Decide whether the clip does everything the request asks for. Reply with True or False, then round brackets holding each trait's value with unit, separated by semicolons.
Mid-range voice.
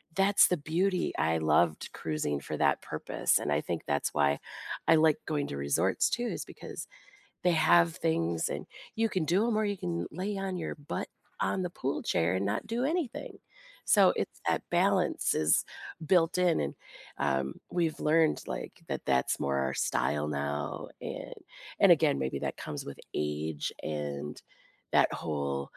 False (85 Hz)